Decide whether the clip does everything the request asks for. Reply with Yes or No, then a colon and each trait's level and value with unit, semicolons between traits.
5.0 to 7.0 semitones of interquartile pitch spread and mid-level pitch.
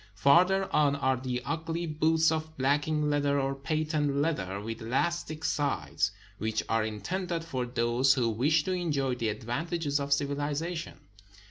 No: average, 4.2 semitones; medium, 145 Hz